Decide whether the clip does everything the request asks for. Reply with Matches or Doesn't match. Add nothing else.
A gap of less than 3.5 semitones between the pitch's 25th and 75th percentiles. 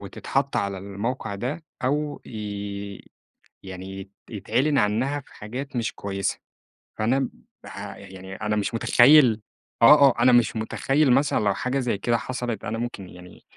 Doesn't match